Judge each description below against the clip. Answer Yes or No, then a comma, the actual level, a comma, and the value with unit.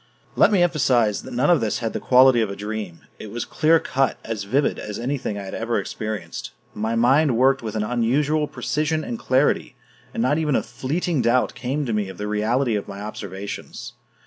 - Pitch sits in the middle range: No, low, 120 Hz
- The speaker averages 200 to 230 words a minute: Yes, fast, 205 wpm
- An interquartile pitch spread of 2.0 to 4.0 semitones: No, average, 4.7 semitones